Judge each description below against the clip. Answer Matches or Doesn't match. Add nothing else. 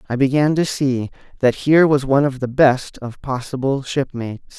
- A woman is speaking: Doesn't match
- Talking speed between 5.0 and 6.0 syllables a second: Matches